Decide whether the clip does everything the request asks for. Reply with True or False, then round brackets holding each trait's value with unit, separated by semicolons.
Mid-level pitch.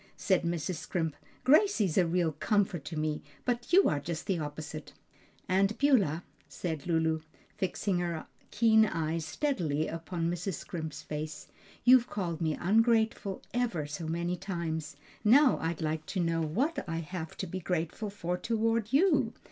True (175 Hz)